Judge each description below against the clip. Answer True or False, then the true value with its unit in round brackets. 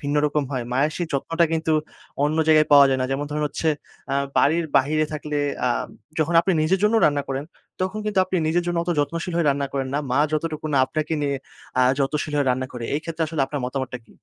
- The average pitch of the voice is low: False (150 Hz)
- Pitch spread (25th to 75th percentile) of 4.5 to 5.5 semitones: False (2.9 semitones)